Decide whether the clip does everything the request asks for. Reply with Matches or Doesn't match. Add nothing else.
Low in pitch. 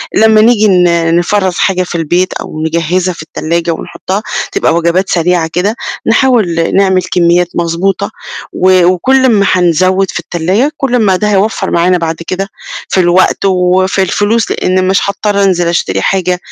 Doesn't match